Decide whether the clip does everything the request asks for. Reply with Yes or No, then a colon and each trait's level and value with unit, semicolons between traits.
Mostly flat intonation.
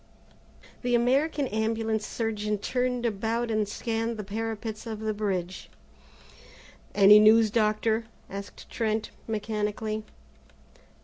Yes: narrow, 1.3 semitones